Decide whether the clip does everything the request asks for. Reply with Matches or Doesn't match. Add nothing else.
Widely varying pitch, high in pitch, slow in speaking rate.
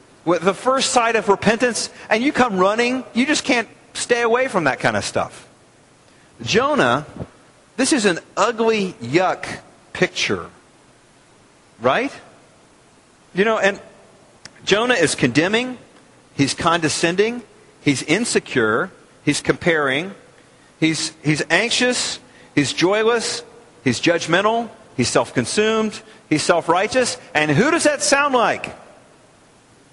Matches